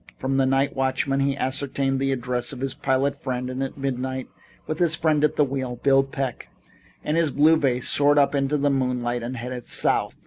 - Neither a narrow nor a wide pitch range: No, narrow, 1.6 semitones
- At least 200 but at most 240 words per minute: Yes, fast, 205 wpm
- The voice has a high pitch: No, low, 135 Hz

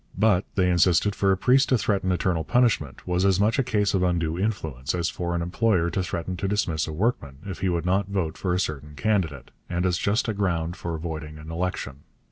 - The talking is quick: Yes, fast, 225 wpm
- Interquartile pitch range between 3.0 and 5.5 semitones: Yes, average, 3.3 semitones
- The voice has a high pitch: No, very low, 90 Hz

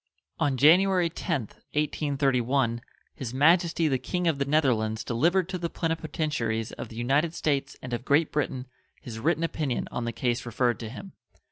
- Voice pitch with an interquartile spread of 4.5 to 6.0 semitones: Yes, average, 5.2 semitones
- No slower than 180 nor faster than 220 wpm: No, average, 165 wpm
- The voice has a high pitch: No, medium, 140 Hz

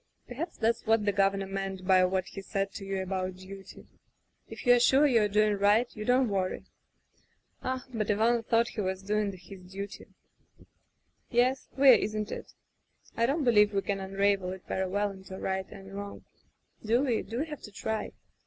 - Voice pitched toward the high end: Yes, high, 205 Hz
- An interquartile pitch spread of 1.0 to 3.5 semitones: Yes, average, 3.1 semitones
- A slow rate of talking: No, average, 190 wpm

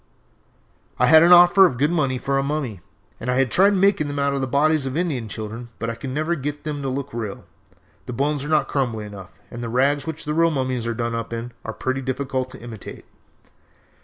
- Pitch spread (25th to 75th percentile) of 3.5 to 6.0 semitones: Yes, average, 4.1 semitones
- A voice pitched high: No, low, 135 Hz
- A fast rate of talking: Yes, fast, 220 wpm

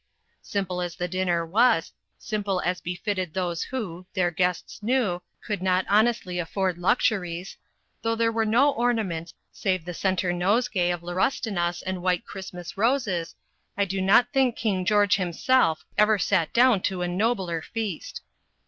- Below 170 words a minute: Yes, average, 150 wpm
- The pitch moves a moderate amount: Yes, average, 3.7 semitones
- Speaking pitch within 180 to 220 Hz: Yes, medium, 185 Hz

